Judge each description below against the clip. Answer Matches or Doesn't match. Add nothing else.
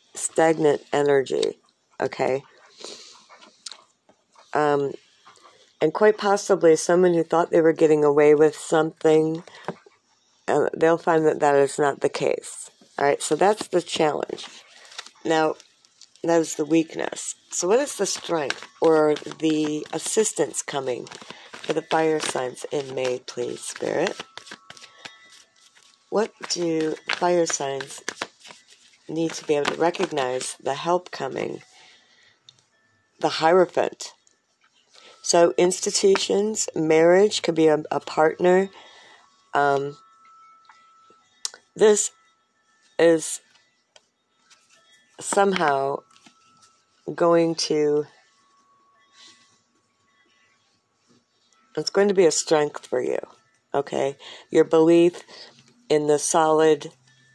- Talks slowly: Matches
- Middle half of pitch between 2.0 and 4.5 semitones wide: Doesn't match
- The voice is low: Doesn't match